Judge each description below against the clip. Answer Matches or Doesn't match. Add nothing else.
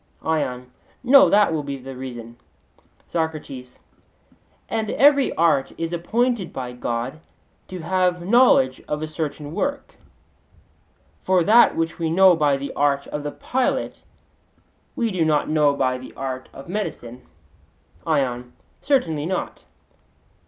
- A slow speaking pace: Matches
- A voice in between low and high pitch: Matches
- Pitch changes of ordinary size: Doesn't match